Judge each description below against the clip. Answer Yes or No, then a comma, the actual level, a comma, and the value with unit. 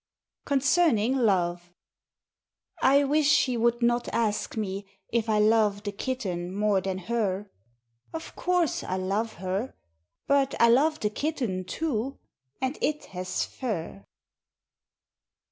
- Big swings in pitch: Yes, wide, 5.7 semitones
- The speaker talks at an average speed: No, slow, 125 wpm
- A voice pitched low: No, high, 225 Hz